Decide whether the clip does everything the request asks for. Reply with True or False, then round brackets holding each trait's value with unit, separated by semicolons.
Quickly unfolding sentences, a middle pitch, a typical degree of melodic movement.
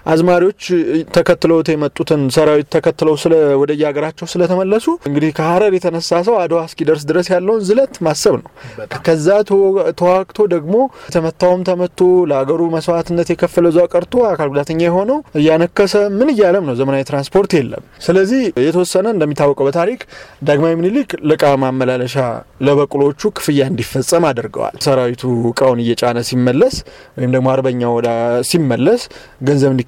True (120 wpm; 165 Hz; 4.2 semitones)